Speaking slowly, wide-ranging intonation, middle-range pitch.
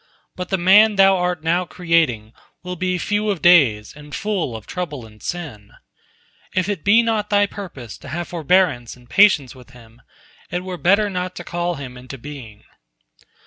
No: average, 180 wpm; wide, 6.7 semitones; medium, 175 Hz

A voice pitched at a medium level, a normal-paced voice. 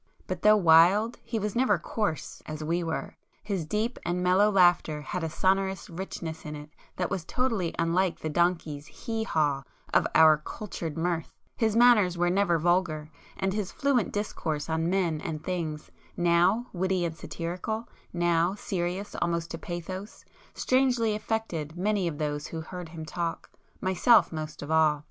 Yes: medium, 175 Hz; average, 160 wpm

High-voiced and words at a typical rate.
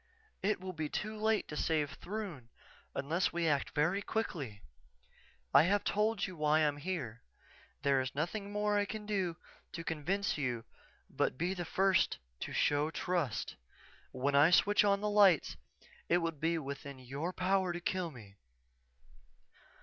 No: medium, 170 Hz; average, 160 wpm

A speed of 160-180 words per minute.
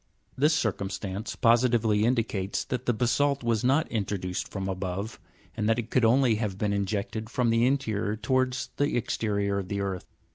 Yes: average, 175 wpm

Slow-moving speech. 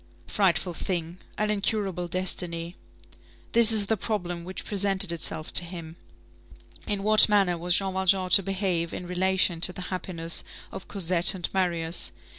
No: average, 150 wpm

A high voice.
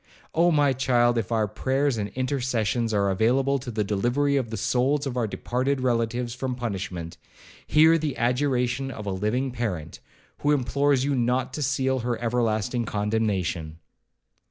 No: low, 125 Hz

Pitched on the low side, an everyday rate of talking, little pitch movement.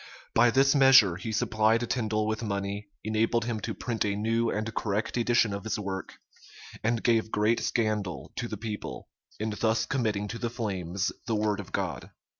Yes: low, 110 Hz; average, 180 wpm; narrow, 2.1 semitones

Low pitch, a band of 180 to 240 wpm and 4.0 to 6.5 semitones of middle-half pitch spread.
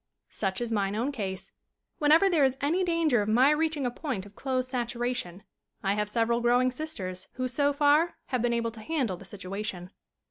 No: high, 245 Hz; average, 190 wpm; wide, 5.6 semitones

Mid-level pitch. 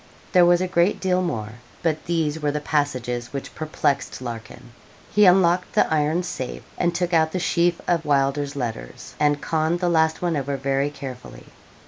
Yes: medium, 155 Hz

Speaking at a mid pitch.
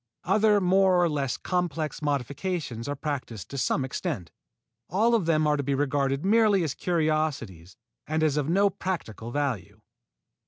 Yes: medium, 150 Hz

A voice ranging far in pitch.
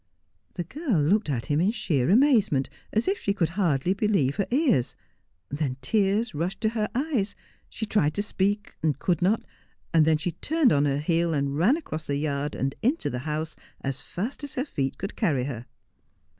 Yes: wide, 6.9 semitones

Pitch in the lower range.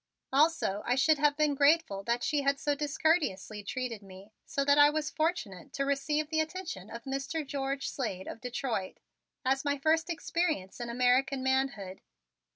No: very high, 275 Hz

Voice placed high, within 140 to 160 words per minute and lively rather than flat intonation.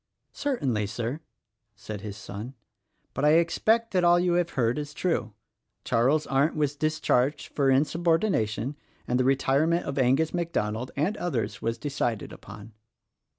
No: medium, 140 Hz; average, 145 wpm; wide, 6.1 semitones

